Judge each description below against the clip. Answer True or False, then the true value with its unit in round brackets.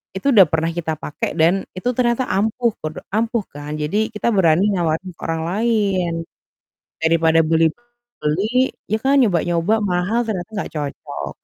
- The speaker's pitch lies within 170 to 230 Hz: True (185 Hz)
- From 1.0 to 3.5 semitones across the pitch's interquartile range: False (5.2 semitones)